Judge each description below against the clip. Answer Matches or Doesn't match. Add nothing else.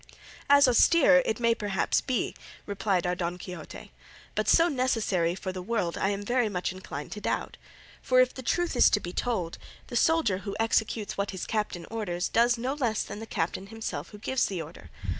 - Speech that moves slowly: Doesn't match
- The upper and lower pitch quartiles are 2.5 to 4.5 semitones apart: Doesn't match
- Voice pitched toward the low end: Doesn't match